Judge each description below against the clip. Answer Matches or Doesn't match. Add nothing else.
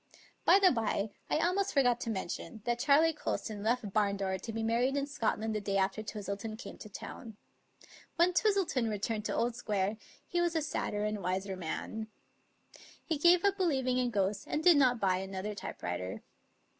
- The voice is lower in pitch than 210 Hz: Doesn't match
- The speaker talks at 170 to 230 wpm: Matches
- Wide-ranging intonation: Matches